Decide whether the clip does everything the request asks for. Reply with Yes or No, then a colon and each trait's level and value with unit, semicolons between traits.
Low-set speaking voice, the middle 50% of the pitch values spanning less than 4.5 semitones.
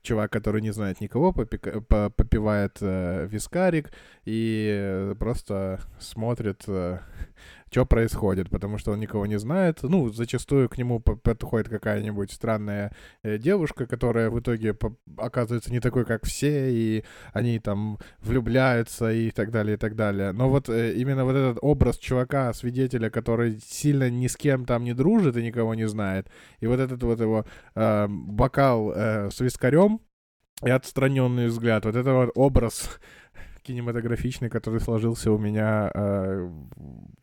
Yes: low, 115 Hz; average, 3.1 semitones